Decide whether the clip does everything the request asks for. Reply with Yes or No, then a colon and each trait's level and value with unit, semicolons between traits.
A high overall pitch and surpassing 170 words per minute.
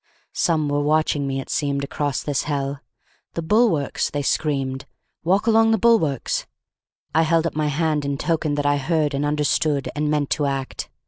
No: medium, 150 Hz; average, 180 wpm